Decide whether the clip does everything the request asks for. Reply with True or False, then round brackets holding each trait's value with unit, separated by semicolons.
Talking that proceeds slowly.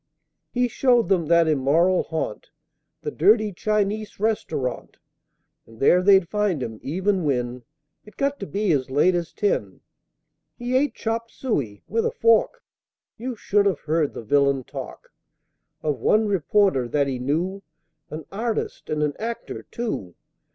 False (150 wpm)